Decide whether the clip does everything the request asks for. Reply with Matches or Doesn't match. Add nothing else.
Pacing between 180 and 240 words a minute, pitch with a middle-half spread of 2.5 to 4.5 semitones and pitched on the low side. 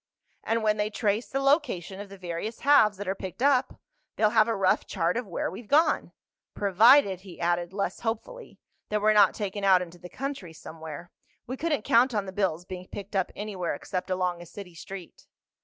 Doesn't match